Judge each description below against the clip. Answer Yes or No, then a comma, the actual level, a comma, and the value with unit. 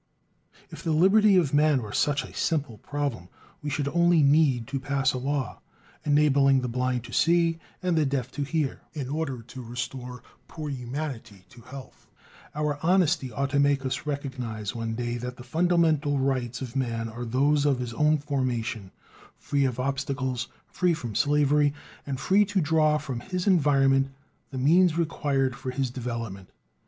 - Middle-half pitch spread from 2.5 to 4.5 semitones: Yes, average, 3.3 semitones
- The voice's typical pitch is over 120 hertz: Yes, medium, 140 Hz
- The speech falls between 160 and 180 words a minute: Yes, average, 170 wpm